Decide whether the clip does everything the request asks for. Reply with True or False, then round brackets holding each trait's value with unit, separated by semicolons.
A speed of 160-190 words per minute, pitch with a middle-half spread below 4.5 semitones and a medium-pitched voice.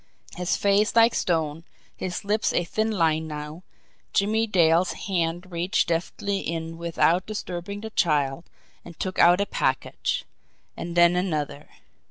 False (140 wpm; 3.3 semitones; 175 Hz)